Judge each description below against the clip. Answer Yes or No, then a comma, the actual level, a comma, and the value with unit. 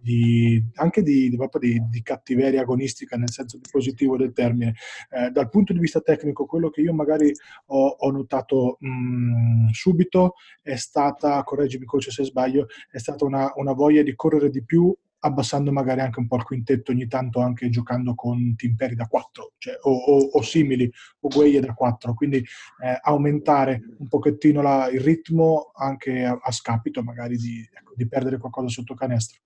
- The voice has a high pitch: No, low, 135 Hz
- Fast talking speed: Yes, fast, 180 wpm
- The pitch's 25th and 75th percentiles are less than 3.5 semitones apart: Yes, average, 2.8 semitones